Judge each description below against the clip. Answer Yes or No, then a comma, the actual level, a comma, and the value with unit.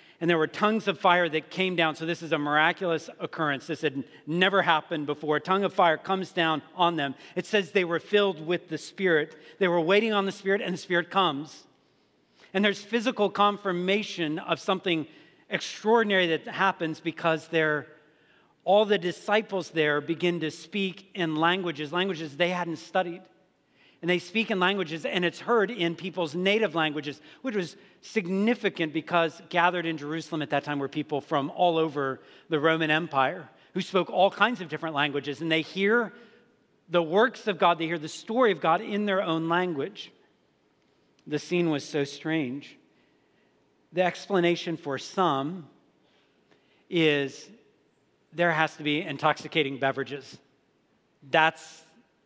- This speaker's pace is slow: No, average, 160 wpm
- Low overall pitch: No, medium, 170 Hz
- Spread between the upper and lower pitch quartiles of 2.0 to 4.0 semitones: Yes, average, 3.5 semitones